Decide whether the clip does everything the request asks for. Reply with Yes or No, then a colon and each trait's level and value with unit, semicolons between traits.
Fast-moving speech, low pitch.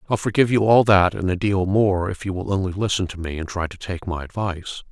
Yes: fast, 270 wpm; very low, 95 Hz